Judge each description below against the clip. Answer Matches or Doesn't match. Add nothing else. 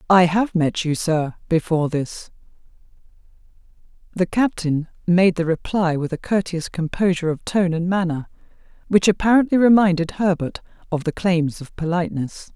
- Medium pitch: Matches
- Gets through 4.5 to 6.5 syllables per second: Matches